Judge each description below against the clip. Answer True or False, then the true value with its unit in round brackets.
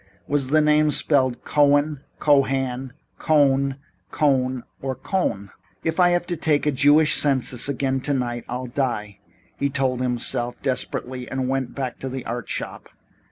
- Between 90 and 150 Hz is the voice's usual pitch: True (135 Hz)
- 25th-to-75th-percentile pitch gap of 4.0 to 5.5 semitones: False (2.4 semitones)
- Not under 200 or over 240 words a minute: False (150 wpm)